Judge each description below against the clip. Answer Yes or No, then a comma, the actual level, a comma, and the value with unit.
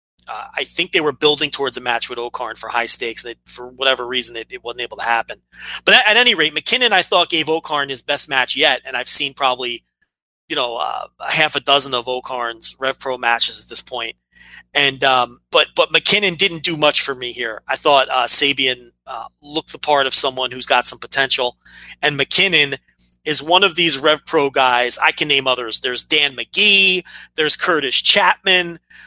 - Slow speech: No, average, 200 wpm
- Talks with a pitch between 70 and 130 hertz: No, medium, 140 Hz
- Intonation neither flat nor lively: Yes, average, 4.2 semitones